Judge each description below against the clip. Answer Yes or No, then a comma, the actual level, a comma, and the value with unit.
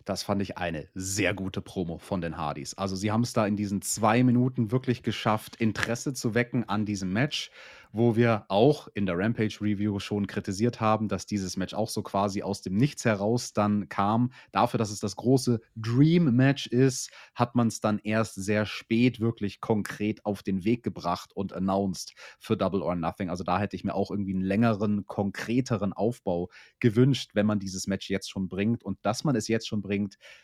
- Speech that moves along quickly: Yes, fast, 200 wpm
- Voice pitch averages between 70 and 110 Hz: Yes, low, 105 Hz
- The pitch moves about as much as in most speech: Yes, average, 3.0 semitones